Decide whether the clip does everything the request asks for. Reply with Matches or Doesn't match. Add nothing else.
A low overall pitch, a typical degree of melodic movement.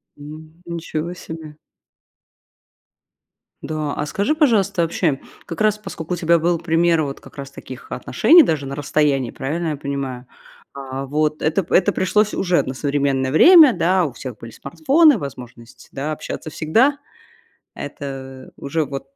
Doesn't match